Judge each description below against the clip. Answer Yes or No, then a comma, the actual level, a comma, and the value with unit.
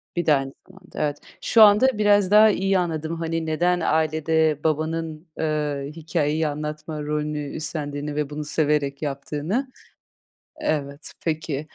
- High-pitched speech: No, medium, 155 Hz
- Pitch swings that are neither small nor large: No, narrow, 1.9 semitones